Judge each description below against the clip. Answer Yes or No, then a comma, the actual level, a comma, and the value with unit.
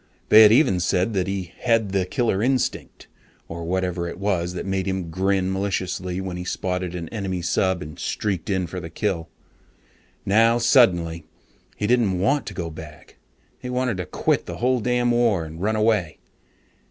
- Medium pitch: No, very low, 95 Hz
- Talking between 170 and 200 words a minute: Yes, average, 180 wpm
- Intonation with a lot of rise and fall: No, average, 3.7 semitones